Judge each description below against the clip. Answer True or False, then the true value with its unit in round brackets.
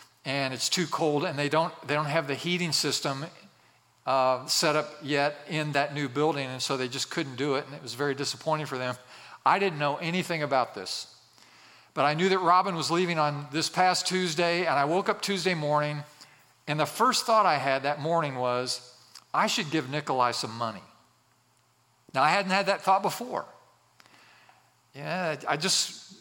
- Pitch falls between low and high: True (150 Hz)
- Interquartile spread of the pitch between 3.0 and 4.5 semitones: True (4.0 semitones)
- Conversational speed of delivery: True (190 wpm)